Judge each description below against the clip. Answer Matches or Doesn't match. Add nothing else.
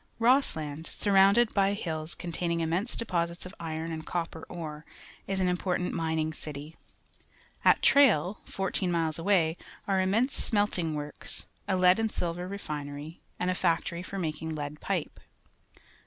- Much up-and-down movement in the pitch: Doesn't match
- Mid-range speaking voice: Matches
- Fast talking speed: Doesn't match